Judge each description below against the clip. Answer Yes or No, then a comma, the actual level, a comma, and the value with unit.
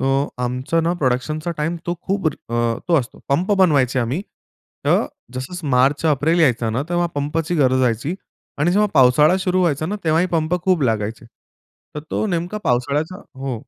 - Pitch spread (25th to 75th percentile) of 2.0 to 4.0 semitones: No, average, 5.1 semitones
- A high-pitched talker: No, medium, 150 Hz